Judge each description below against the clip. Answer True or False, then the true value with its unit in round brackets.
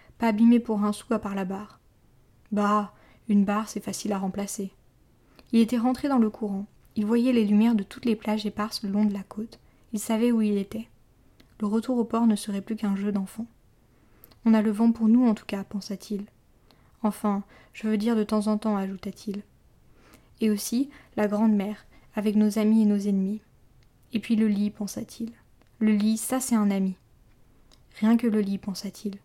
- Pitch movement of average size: False (1.8 semitones)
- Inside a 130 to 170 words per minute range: False (200 wpm)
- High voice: True (210 Hz)